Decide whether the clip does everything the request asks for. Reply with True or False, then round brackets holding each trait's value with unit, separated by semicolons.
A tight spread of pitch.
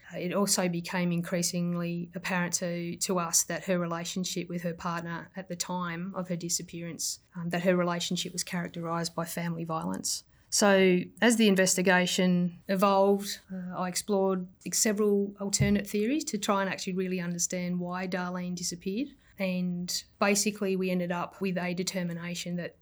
True (1.7 semitones)